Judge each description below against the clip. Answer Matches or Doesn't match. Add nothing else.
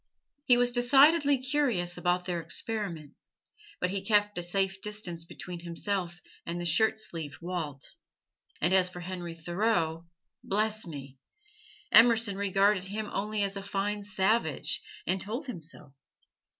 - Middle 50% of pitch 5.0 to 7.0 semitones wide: Doesn't match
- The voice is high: Matches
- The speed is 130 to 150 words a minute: Matches